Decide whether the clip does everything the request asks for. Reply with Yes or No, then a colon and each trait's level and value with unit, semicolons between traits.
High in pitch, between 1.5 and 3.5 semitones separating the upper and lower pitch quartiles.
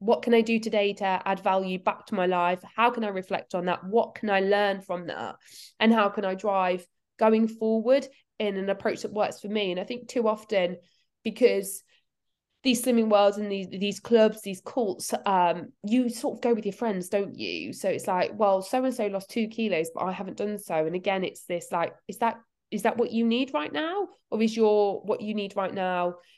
Yes: high, 205 Hz; average, 3.0 semitones